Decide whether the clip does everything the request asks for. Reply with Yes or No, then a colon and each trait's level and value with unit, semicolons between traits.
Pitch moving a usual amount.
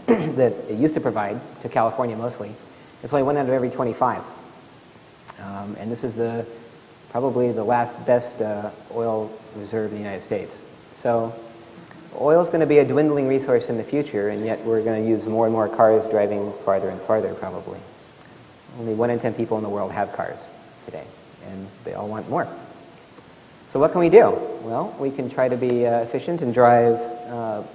No: narrow, 2.3 semitones